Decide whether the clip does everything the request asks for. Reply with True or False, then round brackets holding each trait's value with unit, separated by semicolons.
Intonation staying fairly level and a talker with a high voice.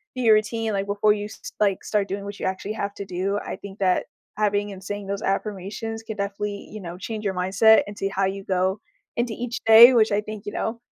True (1.8 semitones; 205 Hz)